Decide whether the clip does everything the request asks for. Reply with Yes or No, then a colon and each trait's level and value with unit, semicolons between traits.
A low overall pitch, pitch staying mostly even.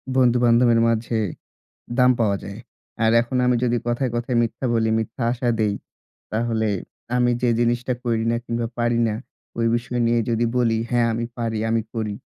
Yes: low, 120 Hz; narrow, 1.3 semitones